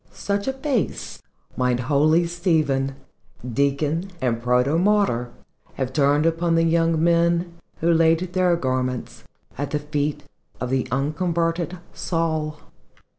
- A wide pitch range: No, average, 3.8 semitones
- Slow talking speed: Yes, slow, 120 wpm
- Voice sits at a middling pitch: Yes, medium, 160 Hz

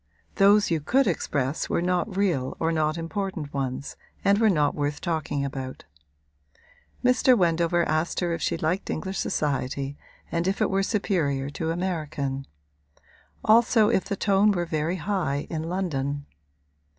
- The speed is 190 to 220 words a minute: No, average, 150 wpm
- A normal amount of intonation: Yes, average, 5.0 semitones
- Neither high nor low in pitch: Yes, medium, 165 Hz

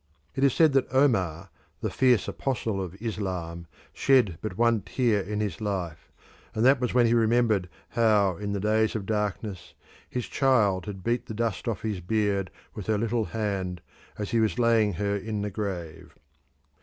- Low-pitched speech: Yes, low, 105 Hz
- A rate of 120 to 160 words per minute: No, average, 180 wpm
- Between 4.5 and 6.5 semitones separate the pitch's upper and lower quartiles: No, average, 3.3 semitones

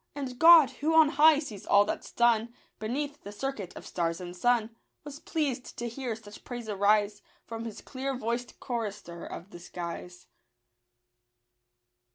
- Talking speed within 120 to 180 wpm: Yes, average, 155 wpm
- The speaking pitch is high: Yes, high, 235 Hz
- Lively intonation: No, average, 4.9 semitones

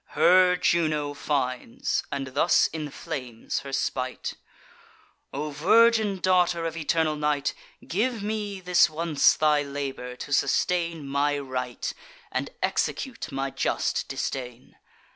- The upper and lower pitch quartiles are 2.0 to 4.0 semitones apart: No, average, 4.5 semitones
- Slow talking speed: Yes, slow, 115 wpm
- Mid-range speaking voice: Yes, medium, 150 Hz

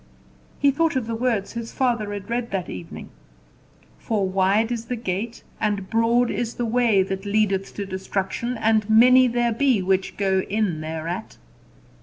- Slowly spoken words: No, average, 165 wpm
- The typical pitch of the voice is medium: No, high, 220 Hz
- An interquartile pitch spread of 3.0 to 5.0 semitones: Yes, average, 3.6 semitones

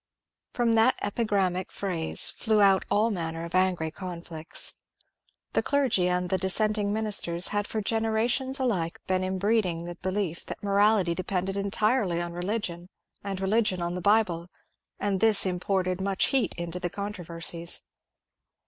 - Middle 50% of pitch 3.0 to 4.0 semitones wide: Yes, average, 3.3 semitones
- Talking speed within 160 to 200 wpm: No, average, 145 wpm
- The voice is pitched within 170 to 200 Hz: Yes, high, 190 Hz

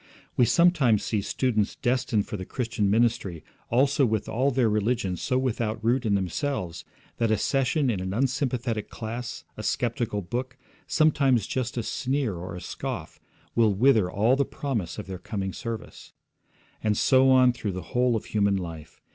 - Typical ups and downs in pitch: Yes, average, 3.9 semitones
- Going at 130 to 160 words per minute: No, average, 170 wpm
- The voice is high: No, low, 115 Hz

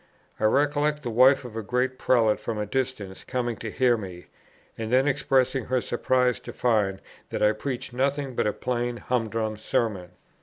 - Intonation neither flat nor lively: Yes, average, 3.1 semitones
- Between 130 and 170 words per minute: No, average, 180 wpm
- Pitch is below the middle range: Yes, low, 120 Hz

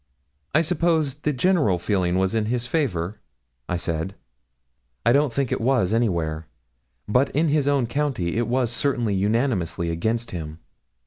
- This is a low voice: Yes, low, 115 Hz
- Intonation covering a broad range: Yes, wide, 7.3 semitones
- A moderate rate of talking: Yes, average, 150 wpm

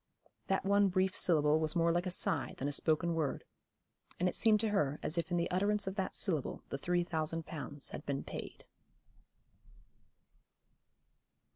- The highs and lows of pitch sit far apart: No, average, 3.6 semitones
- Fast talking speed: No, average, 170 wpm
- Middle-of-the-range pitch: Yes, medium, 170 Hz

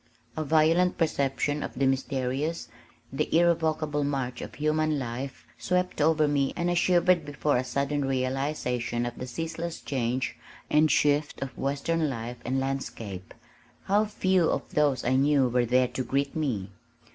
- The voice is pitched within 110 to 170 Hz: Yes, medium, 140 Hz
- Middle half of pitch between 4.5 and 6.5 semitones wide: No, average, 3.4 semitones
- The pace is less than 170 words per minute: Yes, average, 155 wpm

